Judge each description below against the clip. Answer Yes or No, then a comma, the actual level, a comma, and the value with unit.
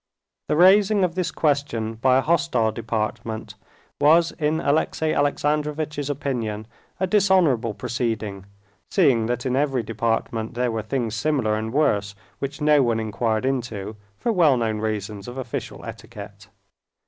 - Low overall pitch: Yes, low, 125 Hz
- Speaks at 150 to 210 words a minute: No, average, 140 wpm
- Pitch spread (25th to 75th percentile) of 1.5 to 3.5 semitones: No, average, 5.2 semitones